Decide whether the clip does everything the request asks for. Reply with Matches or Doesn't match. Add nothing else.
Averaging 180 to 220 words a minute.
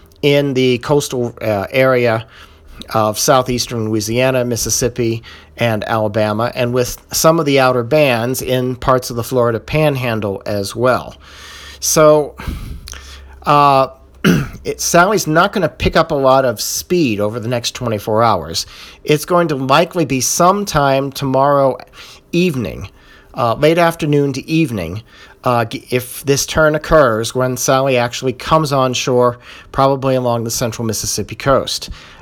Doesn't match